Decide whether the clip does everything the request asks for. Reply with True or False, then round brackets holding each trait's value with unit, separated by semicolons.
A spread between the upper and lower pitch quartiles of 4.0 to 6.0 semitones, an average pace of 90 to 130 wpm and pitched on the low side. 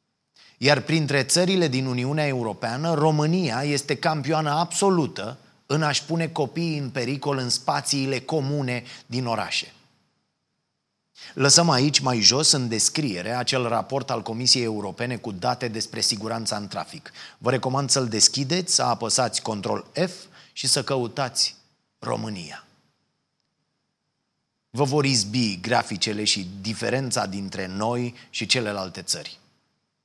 True (4.3 semitones; 120 wpm; 130 Hz)